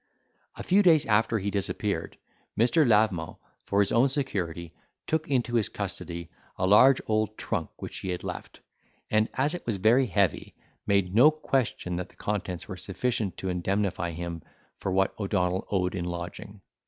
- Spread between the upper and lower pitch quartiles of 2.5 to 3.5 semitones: No, average, 4.5 semitones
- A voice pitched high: No, low, 100 Hz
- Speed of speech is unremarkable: Yes, average, 165 wpm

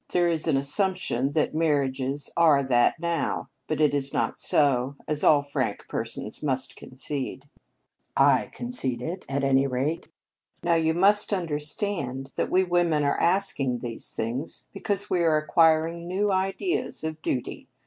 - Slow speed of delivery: No, average, 150 wpm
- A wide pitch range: No, average, 4.2 semitones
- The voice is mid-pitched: Yes, medium, 155 Hz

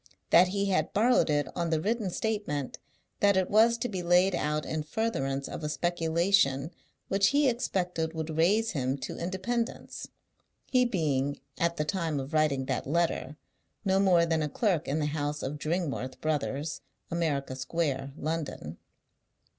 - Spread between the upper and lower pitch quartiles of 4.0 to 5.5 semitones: Yes, average, 4.7 semitones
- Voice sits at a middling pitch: Yes, medium, 165 Hz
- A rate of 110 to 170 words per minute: Yes, average, 160 wpm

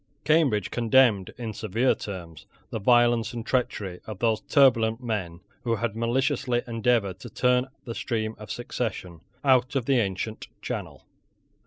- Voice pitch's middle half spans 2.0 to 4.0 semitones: Yes, average, 2.8 semitones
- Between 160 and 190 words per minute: No, average, 145 wpm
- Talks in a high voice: No, low, 115 Hz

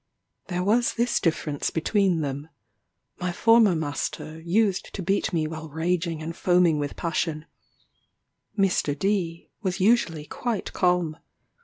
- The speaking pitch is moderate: Yes, medium, 175 Hz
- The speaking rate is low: Yes, slow, 130 wpm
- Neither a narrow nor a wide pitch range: Yes, average, 3.6 semitones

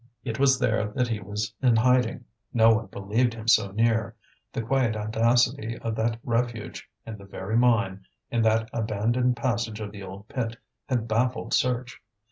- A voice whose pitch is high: No, low, 115 Hz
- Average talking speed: Yes, average, 170 wpm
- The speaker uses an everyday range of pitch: No, narrow, 2.0 semitones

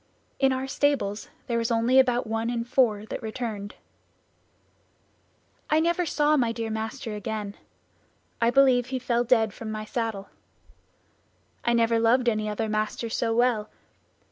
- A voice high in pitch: Yes, high, 230 Hz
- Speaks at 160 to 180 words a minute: No, average, 145 wpm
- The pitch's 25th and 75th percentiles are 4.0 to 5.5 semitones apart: No, narrow, 2.5 semitones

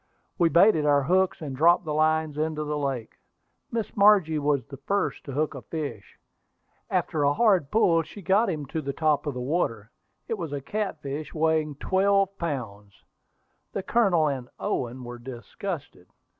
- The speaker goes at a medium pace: Yes, average, 170 wpm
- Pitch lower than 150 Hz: No, medium, 155 Hz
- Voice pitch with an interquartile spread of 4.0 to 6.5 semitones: Yes, average, 4.3 semitones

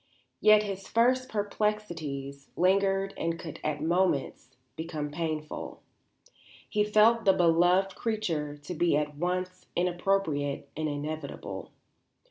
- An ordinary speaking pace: No, slow, 110 wpm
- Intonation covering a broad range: No, average, 4.5 semitones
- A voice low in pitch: No, medium, 175 Hz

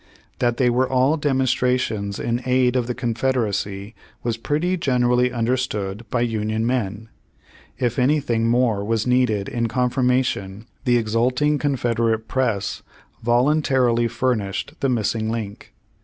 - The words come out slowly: Yes, slow, 125 wpm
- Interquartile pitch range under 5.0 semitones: Yes, narrow, 2.5 semitones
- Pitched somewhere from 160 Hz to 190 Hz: No, low, 120 Hz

